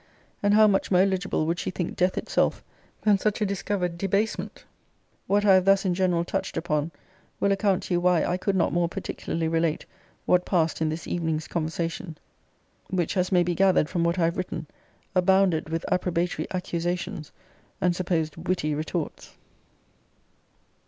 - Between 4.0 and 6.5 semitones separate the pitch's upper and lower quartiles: No, narrow, 2.4 semitones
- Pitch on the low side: No, medium, 180 Hz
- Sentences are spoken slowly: No, average, 165 wpm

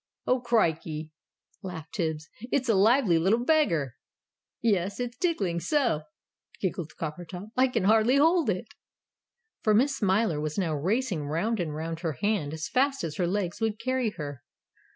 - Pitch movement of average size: No, wide, 6.7 semitones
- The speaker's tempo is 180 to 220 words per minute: No, average, 155 wpm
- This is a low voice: No, high, 195 Hz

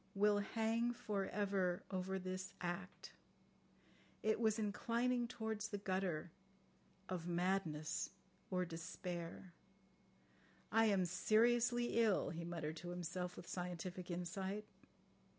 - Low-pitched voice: No, high, 190 Hz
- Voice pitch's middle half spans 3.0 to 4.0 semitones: Yes, average, 3.5 semitones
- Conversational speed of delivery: No, slow, 115 wpm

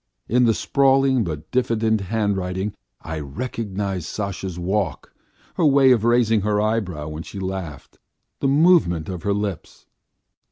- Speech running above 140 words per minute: No, slow, 135 wpm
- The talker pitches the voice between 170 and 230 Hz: No, low, 105 Hz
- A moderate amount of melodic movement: Yes, average, 4.5 semitones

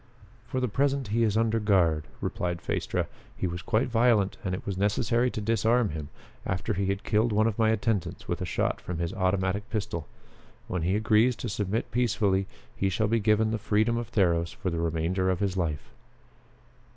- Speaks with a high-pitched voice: No, low, 105 Hz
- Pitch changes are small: No, average, 3.5 semitones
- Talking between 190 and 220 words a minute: Yes, average, 195 wpm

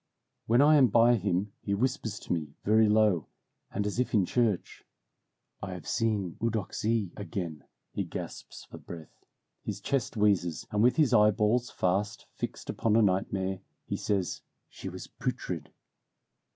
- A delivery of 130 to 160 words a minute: Yes, average, 150 wpm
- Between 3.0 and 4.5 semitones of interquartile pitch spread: Yes, average, 3.4 semitones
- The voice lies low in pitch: Yes, low, 105 Hz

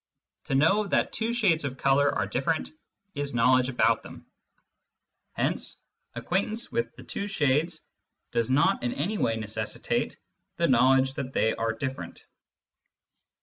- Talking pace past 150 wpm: No, average, 140 wpm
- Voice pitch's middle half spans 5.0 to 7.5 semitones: Yes, average, 5.3 semitones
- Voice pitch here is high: No, medium, 140 Hz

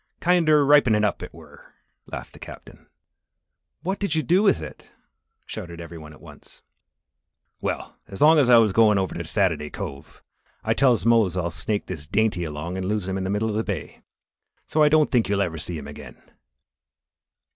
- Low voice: Yes, low, 105 Hz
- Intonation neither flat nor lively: No, wide, 6.6 semitones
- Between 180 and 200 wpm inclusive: Yes, average, 185 wpm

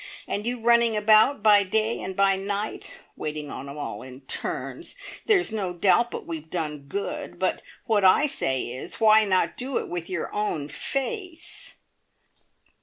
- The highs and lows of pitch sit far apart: Yes, wide, 5.9 semitones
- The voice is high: Yes, high, 200 Hz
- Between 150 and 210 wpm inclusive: Yes, average, 165 wpm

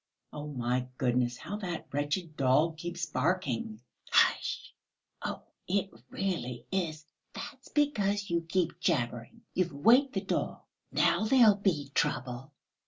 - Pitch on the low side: No, medium, 165 Hz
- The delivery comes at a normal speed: No, slow, 130 wpm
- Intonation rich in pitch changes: Yes, wide, 6.8 semitones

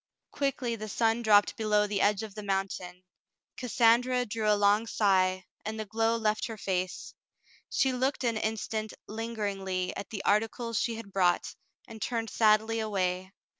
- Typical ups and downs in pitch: No, narrow, 2.3 semitones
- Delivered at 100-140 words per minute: No, average, 165 wpm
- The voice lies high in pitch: Yes, high, 215 Hz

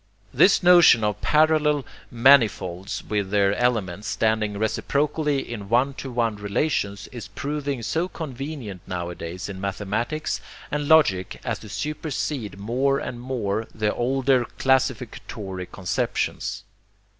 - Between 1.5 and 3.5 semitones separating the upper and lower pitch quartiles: No, wide, 5.6 semitones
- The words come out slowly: Yes, slow, 120 wpm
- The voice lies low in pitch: Yes, low, 120 Hz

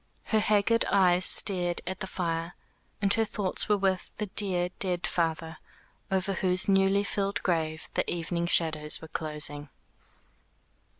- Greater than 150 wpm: No, average, 140 wpm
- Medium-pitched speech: Yes, medium, 180 Hz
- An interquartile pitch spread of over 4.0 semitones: No, average, 3.1 semitones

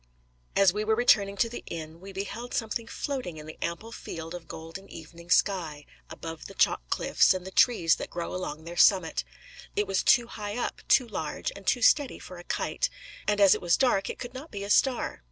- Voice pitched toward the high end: Yes, high, 195 Hz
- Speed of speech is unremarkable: No, fast, 215 wpm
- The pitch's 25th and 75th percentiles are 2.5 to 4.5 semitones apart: No, average, 5.2 semitones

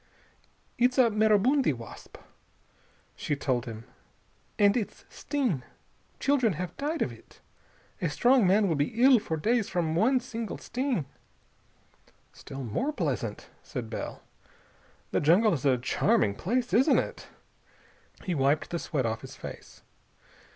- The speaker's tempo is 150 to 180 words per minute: No, slow, 135 wpm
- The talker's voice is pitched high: Yes, high, 205 Hz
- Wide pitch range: Yes, wide, 8.8 semitones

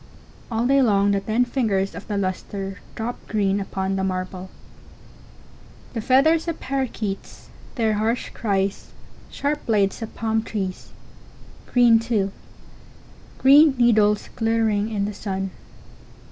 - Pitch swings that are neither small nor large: Yes, average, 3.5 semitones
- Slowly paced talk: Yes, slow, 115 wpm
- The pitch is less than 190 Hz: No, high, 215 Hz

